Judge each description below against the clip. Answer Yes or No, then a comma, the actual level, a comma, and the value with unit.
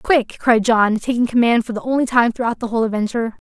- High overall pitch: Yes, high, 235 Hz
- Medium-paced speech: No, fast, 225 wpm